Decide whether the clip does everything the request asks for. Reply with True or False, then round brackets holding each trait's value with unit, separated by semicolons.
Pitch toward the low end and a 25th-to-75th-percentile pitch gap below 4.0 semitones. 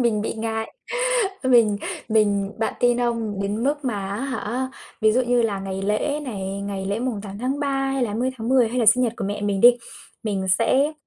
False (225 Hz; 3.6 semitones)